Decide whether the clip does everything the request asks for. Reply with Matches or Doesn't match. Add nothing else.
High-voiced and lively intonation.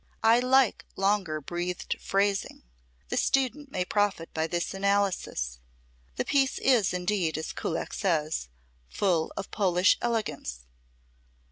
Doesn't match